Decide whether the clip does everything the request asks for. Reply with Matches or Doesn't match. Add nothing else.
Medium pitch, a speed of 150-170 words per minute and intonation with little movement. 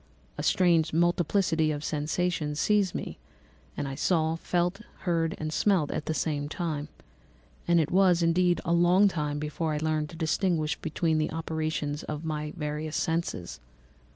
Matches